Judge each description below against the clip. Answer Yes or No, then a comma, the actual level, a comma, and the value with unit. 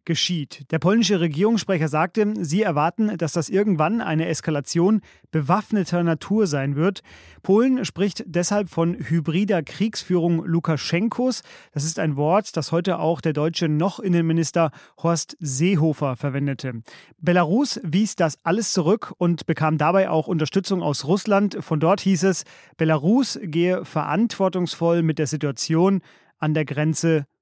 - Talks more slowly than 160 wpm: Yes, average, 135 wpm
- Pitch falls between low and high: Yes, medium, 170 Hz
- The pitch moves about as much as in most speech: Yes, average, 3.6 semitones